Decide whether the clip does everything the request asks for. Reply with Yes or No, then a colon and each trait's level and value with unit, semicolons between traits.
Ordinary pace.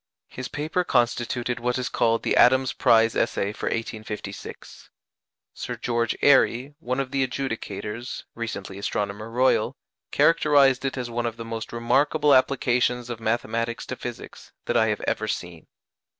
Yes: average, 150 wpm